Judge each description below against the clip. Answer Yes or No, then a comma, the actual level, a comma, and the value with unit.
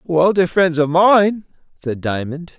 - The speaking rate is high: No, average, 165 wpm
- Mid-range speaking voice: Yes, medium, 170 Hz